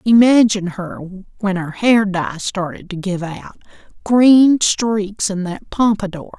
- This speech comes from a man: No, female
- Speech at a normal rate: No, slow, 130 wpm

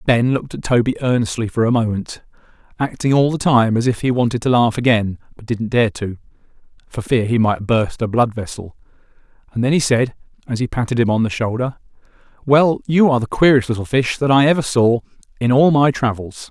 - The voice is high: No, low, 120 Hz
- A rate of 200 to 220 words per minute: Yes, fast, 205 wpm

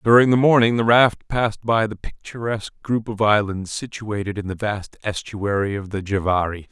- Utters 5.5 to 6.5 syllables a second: No, 5.1 syllables/s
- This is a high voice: No, low, 105 Hz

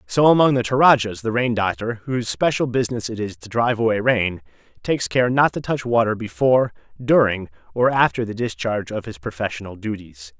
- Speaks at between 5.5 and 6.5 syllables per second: Yes, 5.8 syllables/s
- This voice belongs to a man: Yes, male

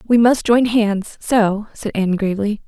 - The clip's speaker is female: Yes, female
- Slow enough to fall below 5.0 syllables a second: Yes, 4.5 syllables/s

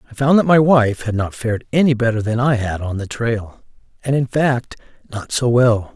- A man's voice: Yes, male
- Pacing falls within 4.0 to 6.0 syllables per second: Yes, 5.1 syllables/s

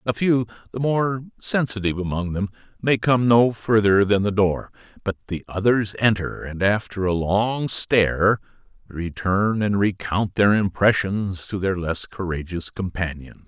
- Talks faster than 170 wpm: No, average, 145 wpm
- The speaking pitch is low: Yes, low, 100 Hz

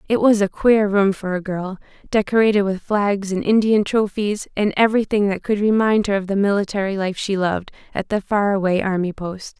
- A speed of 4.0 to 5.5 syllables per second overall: Yes, 5.4 syllables/s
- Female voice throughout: Yes, female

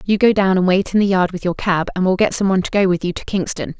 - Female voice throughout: Yes, female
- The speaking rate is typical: No, fast, 350 wpm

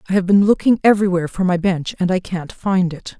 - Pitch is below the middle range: No, medium, 185 Hz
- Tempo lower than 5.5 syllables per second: No, 6.2 syllables/s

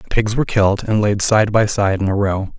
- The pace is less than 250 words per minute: No, fast, 280 wpm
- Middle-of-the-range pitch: No, low, 105 Hz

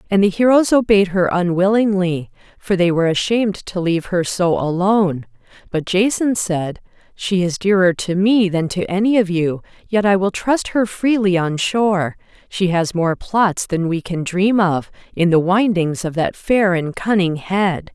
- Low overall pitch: No, medium, 185 Hz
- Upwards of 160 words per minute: Yes, average, 180 wpm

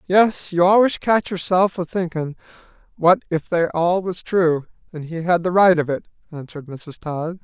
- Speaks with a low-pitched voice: No, medium, 175 Hz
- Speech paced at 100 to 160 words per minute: No, average, 185 wpm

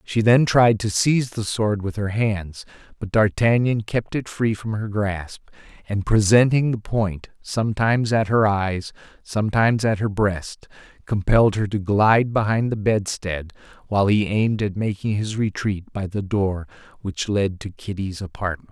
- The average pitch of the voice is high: No, low, 105 Hz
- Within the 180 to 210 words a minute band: No, average, 165 wpm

